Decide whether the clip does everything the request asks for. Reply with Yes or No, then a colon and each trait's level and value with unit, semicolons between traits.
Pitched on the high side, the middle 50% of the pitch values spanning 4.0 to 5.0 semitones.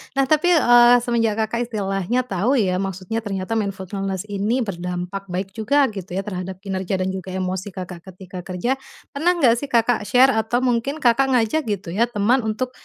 Yes: high, 210 Hz; average, 4.3 semitones